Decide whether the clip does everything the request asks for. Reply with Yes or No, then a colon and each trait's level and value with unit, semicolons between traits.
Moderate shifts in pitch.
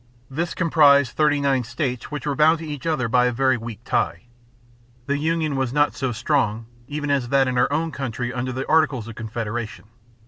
Yes: average, 3.5 semitones